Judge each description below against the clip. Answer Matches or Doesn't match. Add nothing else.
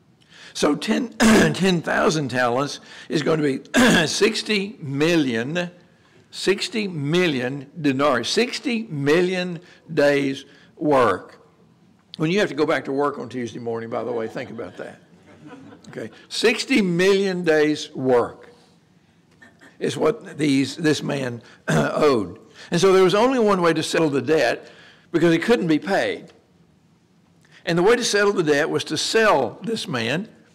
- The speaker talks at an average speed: Matches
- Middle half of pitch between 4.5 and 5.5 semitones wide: Matches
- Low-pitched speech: Doesn't match